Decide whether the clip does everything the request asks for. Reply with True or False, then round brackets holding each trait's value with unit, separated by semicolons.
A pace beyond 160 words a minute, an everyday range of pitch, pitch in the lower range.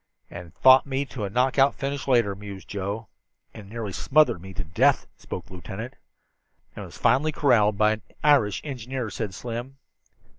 True (170 wpm; 4.7 semitones; 115 Hz)